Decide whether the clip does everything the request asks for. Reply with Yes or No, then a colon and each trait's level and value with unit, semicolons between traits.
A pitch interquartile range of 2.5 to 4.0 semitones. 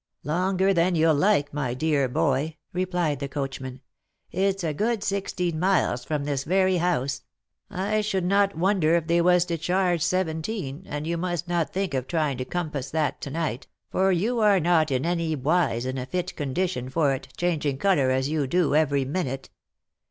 No: average, 4.4 semitones